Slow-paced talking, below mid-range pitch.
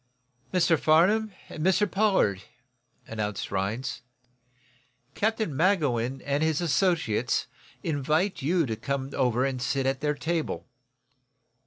No: slow, 115 wpm; medium, 150 Hz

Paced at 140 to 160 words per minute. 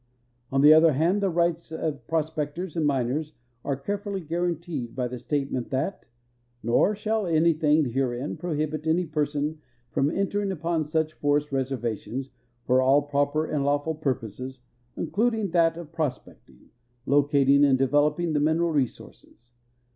Yes: average, 145 wpm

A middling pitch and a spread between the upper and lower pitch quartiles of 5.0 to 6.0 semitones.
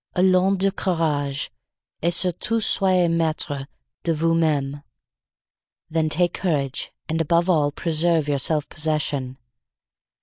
No: medium, 160 Hz; average, 3.2 semitones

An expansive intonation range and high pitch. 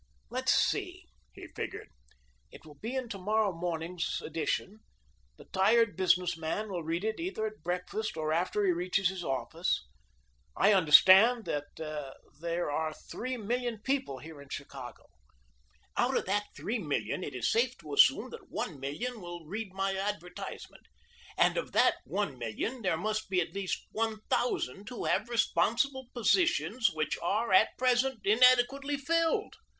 Yes: wide, 6.1 semitones; high, 195 Hz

